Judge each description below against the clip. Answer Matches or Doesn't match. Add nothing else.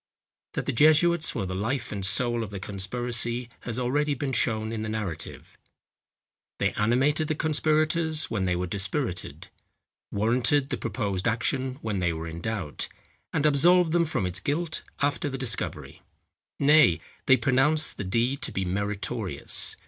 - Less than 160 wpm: Matches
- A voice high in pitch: Doesn't match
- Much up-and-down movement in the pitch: Matches